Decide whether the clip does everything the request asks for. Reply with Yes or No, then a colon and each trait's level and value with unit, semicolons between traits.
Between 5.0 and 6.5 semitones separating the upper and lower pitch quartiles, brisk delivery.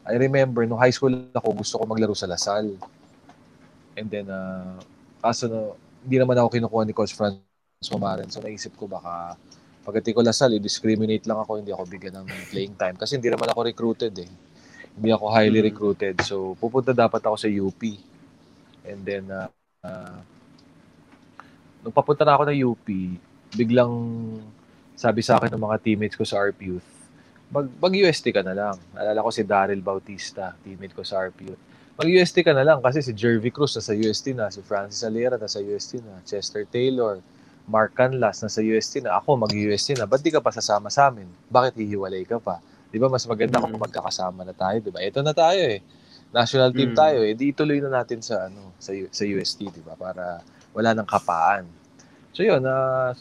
No: average, 3.9 semitones; fast, 195 wpm